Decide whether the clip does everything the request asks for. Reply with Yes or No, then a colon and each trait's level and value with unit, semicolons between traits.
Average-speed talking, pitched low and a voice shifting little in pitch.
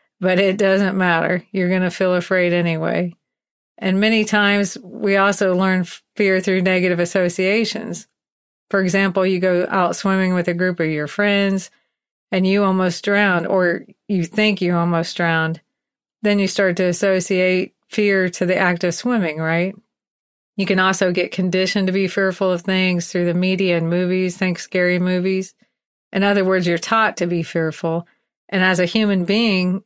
No: average, 170 wpm; medium, 185 Hz; narrow, 1.6 semitones